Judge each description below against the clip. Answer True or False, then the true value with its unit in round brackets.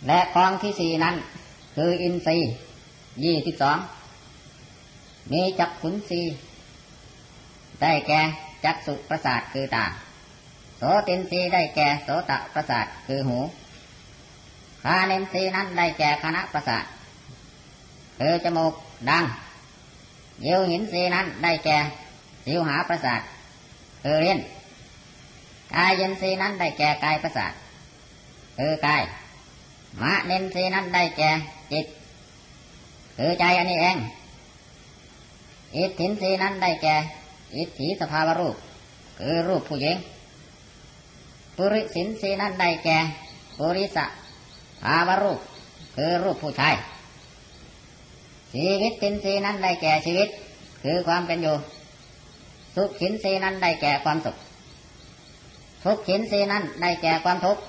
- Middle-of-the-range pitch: True (165 Hz)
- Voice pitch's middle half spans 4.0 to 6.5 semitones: False (3.4 semitones)